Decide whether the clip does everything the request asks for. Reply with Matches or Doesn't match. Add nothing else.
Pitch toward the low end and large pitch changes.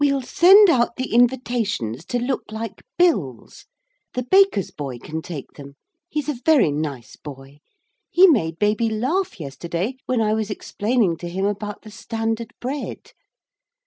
Doesn't match